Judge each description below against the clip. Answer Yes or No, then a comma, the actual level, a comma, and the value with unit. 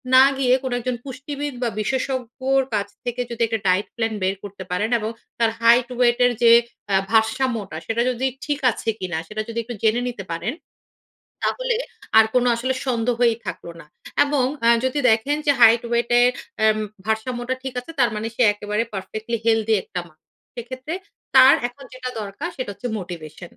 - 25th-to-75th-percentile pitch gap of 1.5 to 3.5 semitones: Yes, average, 3.0 semitones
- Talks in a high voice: Yes, high, 235 Hz